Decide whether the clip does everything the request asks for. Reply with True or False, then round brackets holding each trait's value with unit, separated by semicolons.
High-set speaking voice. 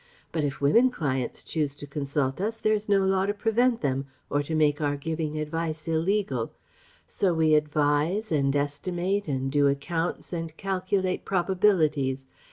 False (160 Hz)